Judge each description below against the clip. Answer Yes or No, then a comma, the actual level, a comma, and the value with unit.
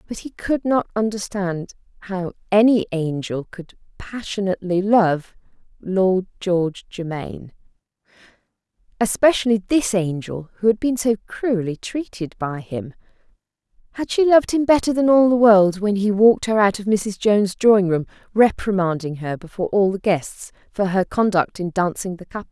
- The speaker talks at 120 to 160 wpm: Yes, average, 150 wpm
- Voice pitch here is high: Yes, high, 200 Hz